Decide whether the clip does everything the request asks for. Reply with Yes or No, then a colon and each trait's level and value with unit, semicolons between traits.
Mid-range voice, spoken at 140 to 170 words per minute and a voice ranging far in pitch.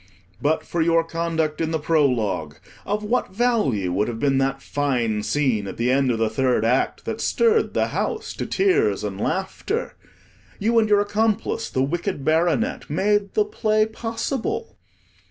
Yes: medium, 160 Hz; average, 165 wpm; wide, 8.7 semitones